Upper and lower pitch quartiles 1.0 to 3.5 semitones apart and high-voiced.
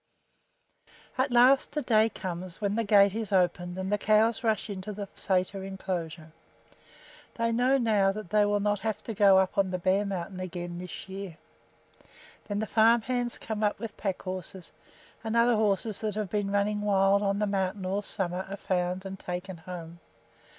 Yes: narrow, 2.5 semitones; high, 200 Hz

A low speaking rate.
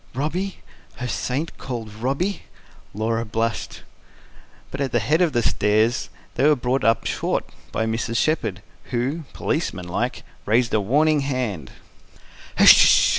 Yes: slow, 130 wpm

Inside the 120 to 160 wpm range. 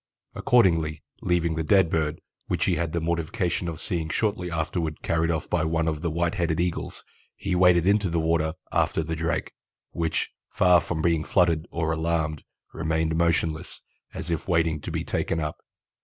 No: average, 175 wpm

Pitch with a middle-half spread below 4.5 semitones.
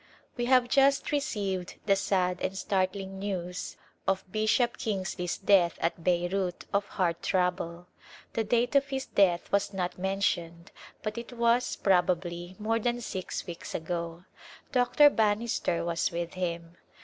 Yes: average, 4.1 semitones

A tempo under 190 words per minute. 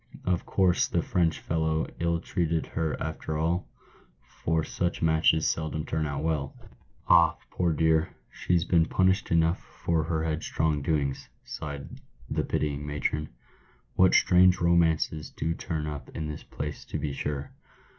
Yes: average, 150 wpm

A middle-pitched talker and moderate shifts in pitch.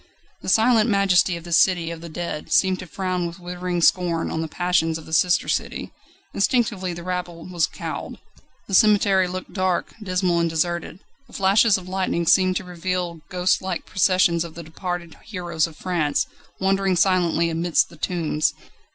No: medium, 180 Hz; narrow, 1.8 semitones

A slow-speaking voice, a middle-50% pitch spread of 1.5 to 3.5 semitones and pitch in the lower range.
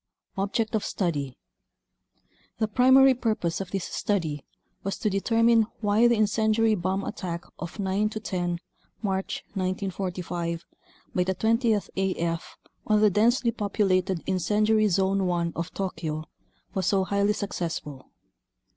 No: slow, 125 wpm; average, 3.2 semitones; high, 195 Hz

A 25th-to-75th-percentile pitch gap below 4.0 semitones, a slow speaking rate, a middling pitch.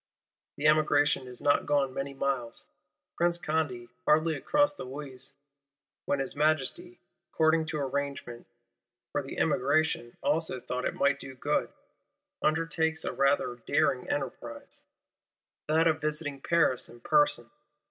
Yes: average, 3.1 semitones; slow, 125 wpm; medium, 145 Hz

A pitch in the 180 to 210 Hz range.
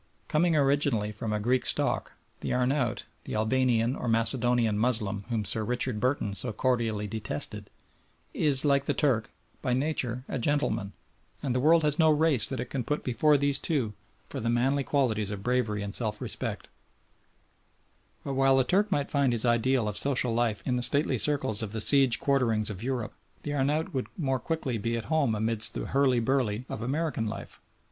No: low, 125 Hz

